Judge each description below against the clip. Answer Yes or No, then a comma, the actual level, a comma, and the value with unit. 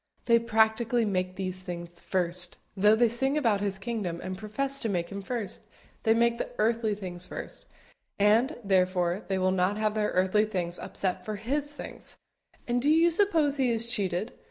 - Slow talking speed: No, average, 180 wpm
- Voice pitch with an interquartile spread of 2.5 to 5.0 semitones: Yes, average, 4.1 semitones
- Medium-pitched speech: No, high, 210 Hz